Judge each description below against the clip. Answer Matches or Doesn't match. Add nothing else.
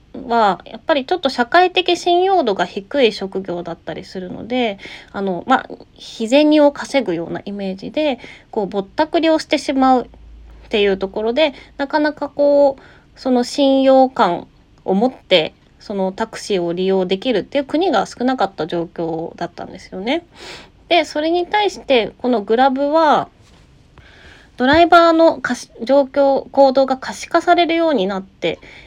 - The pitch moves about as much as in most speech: Doesn't match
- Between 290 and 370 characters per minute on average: Matches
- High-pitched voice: Matches